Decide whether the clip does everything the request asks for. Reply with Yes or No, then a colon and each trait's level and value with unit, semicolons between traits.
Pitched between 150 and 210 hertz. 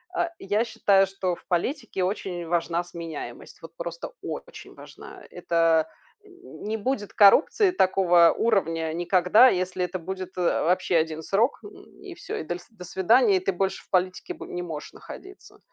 Yes: medium, 185 Hz